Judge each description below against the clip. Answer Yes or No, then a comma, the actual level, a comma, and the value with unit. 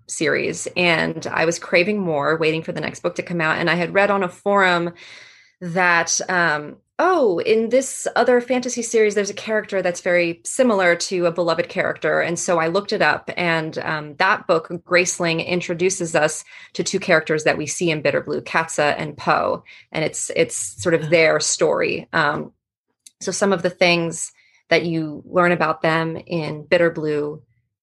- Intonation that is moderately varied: Yes, average, 3.0 semitones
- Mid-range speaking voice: Yes, medium, 175 Hz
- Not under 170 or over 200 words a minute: Yes, average, 185 wpm